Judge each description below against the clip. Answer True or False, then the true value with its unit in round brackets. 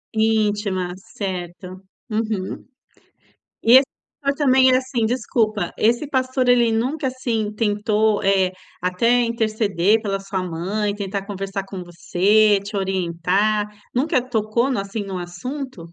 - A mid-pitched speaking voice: False (215 Hz)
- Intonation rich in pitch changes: False (3.5 semitones)